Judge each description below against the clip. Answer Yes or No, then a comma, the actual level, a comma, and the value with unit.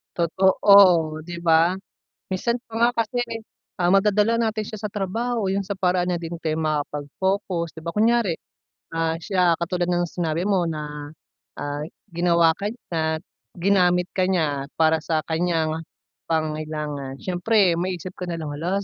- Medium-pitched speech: Yes, medium, 175 Hz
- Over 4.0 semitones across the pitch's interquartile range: No, average, 3.4 semitones